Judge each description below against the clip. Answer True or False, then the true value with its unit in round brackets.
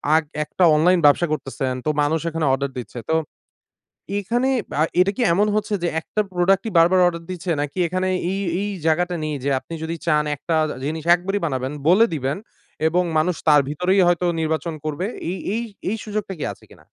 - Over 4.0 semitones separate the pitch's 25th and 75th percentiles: False (3.5 semitones)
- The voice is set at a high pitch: False (170 Hz)